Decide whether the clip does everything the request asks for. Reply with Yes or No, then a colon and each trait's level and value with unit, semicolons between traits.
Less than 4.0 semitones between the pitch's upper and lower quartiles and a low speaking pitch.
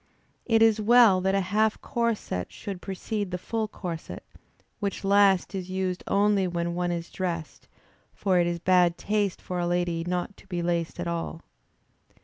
No: average, 2.8 semitones; medium, 185 Hz